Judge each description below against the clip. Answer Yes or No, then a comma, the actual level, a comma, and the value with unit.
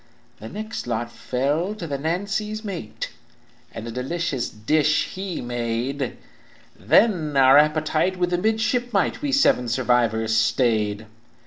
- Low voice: No, medium, 150 Hz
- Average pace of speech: No, slow, 125 wpm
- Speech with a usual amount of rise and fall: No, wide, 7.8 semitones